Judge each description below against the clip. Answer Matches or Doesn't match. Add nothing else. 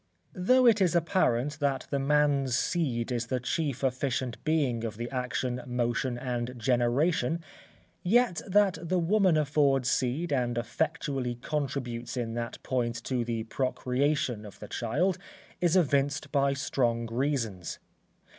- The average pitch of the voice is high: Doesn't match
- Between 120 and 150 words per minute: Matches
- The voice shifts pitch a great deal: Doesn't match